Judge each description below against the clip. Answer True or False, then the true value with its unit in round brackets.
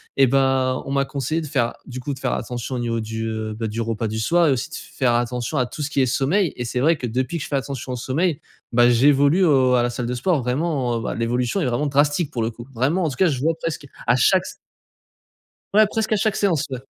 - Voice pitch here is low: True (130 Hz)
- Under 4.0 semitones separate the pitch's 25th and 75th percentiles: True (3.6 semitones)